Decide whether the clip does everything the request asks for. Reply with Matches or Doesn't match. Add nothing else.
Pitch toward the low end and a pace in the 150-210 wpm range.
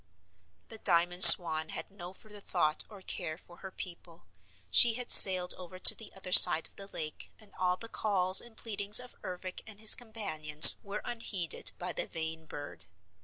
Doesn't match